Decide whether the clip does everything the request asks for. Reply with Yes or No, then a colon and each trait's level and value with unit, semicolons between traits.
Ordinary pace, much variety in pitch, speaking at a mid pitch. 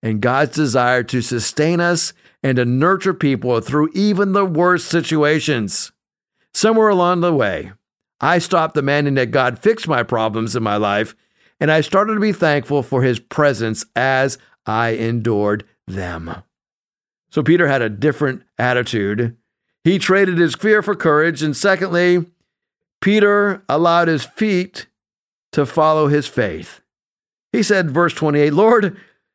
Yes: average, 145 wpm; wide, 6.3 semitones; medium, 150 Hz